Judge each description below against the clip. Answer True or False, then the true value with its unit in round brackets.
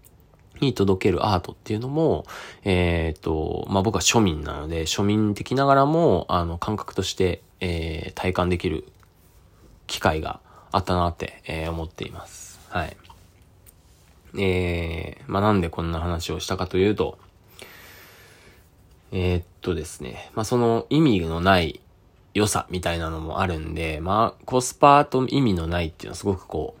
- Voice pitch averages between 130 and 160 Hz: False (90 Hz)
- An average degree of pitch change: True (3.6 semitones)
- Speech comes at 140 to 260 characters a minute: False (305 characters per minute)